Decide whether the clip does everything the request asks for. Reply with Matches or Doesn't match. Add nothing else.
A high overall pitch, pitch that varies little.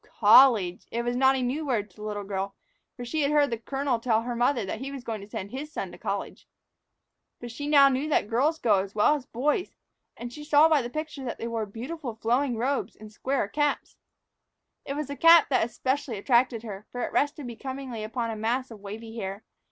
Doesn't match